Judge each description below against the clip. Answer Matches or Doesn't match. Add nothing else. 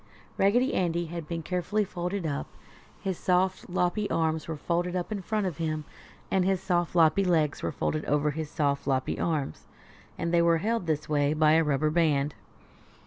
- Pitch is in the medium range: Matches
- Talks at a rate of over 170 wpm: Matches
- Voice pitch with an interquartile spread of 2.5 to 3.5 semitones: Matches